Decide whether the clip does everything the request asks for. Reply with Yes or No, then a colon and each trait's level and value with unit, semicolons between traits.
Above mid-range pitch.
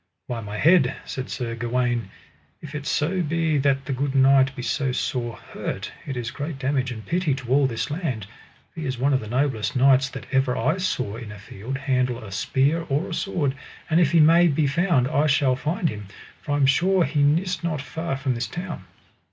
No: low, 135 Hz